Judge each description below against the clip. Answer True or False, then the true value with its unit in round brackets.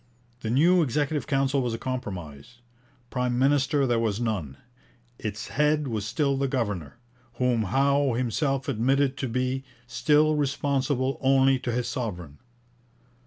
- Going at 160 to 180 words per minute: False (135 wpm)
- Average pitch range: True (3.4 semitones)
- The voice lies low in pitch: True (130 Hz)